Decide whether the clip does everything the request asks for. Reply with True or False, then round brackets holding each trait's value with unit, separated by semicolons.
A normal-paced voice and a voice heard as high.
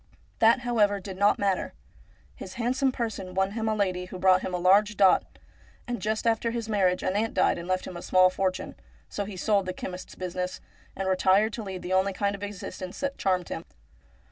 False (215 wpm; 195 Hz)